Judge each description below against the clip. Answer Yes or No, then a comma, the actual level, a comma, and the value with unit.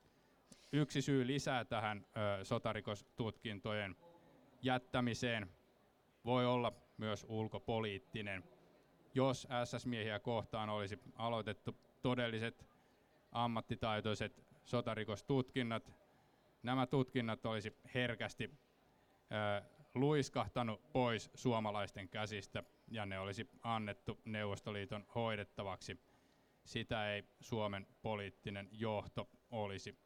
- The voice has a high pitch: No, low, 115 Hz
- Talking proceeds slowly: Yes, slow, 75 wpm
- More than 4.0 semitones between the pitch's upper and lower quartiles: No, average, 3.0 semitones